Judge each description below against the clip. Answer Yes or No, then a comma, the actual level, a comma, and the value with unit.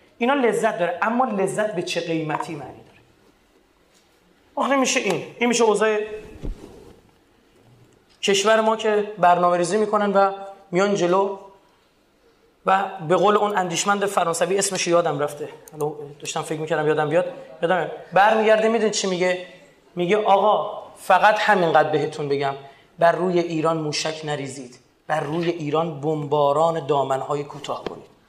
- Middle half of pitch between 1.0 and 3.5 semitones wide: No, average, 5.1 semitones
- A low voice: No, medium, 180 Hz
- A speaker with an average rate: Yes, average, 130 wpm